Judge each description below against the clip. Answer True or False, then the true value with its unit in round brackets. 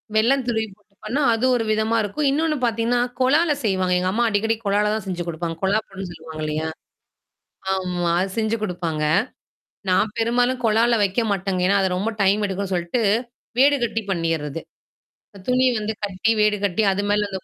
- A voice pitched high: True (205 Hz)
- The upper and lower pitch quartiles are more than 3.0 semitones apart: True (3.7 semitones)